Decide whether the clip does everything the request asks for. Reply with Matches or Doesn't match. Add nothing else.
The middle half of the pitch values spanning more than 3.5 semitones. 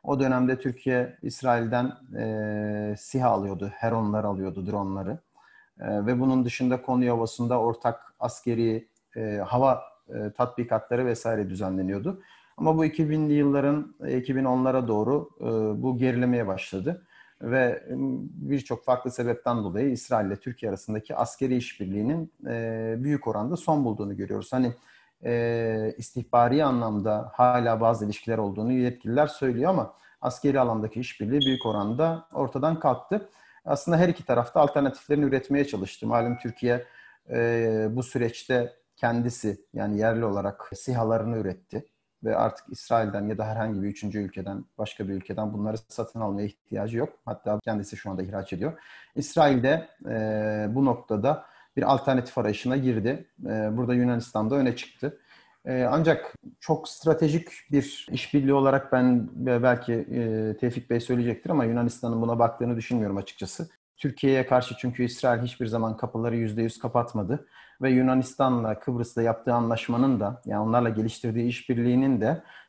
Doesn't match